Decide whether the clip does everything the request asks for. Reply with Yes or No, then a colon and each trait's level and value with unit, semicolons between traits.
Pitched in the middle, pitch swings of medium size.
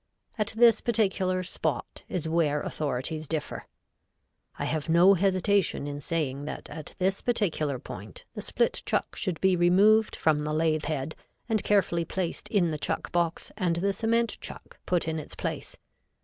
Yes: medium, 170 Hz; average, 4.1 semitones